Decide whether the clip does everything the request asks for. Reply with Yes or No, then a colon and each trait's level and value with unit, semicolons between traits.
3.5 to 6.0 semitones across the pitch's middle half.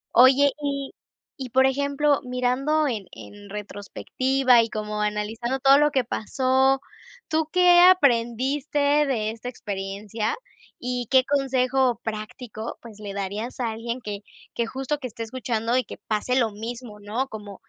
Yes: average, 3.8 semitones